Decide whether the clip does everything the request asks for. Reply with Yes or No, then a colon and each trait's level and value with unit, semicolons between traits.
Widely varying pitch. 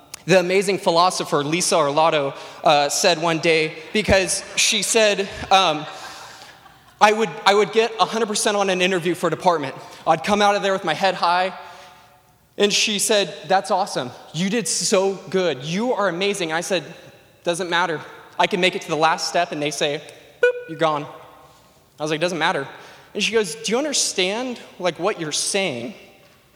No: average, 3.8 semitones